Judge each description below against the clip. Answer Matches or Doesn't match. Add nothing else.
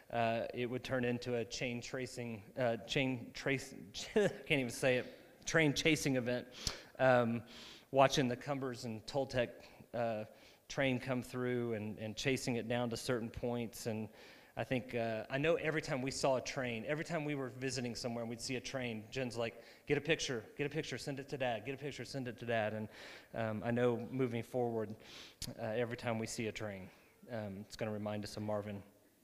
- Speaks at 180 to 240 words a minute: Matches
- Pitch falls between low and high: Doesn't match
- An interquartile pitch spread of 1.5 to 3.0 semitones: Matches